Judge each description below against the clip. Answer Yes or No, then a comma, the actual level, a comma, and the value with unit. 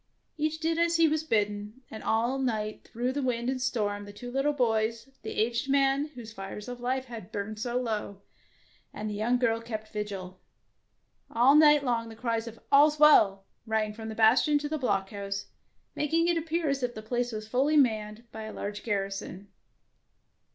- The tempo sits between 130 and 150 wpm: No, average, 190 wpm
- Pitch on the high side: Yes, high, 230 Hz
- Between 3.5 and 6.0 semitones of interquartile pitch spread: Yes, average, 4.2 semitones